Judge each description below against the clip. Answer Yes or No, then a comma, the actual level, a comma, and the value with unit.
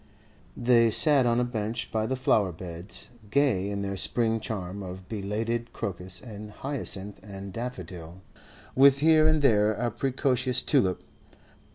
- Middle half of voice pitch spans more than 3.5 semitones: Yes, average, 4.4 semitones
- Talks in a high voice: No, low, 110 Hz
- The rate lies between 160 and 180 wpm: No, average, 145 wpm